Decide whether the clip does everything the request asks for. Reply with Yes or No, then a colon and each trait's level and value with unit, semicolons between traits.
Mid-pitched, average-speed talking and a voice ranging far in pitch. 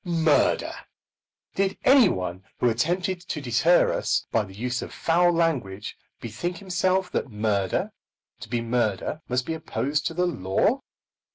Yes: medium, 150 Hz; average, 150 wpm; wide, 7.8 semitones